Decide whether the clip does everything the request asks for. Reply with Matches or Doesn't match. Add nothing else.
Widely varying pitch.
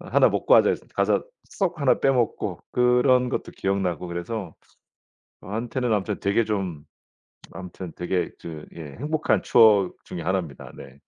Matches